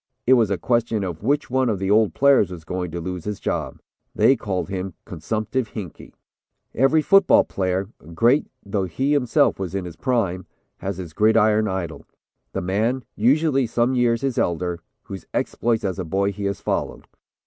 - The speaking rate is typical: Yes, average, 180 wpm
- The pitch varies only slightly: No, average, 4.8 semitones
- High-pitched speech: No, low, 105 Hz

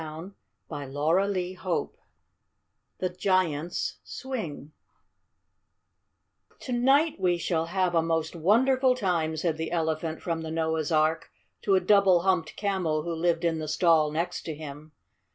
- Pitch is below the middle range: No, medium, 170 Hz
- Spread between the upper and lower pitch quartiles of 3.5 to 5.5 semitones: No, average, 2.9 semitones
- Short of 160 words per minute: Yes, average, 145 wpm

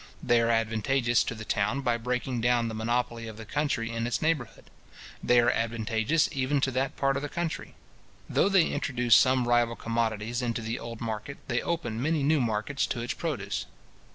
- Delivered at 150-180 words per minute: No, average, 190 wpm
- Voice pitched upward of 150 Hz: No, low, 120 Hz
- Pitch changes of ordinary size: Yes, average, 3.1 semitones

